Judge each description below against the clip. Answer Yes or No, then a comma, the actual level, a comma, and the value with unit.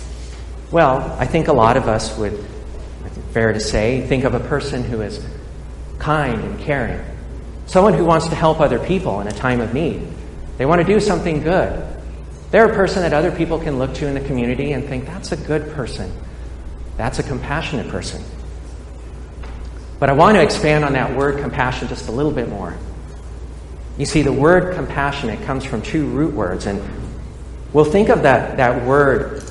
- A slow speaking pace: No, average, 185 wpm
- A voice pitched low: Yes, low, 125 Hz